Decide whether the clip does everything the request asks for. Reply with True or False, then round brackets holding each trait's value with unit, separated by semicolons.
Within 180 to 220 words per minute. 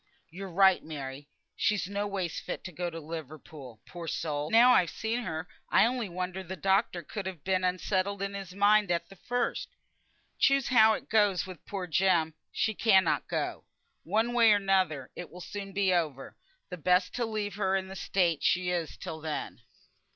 True (190 wpm)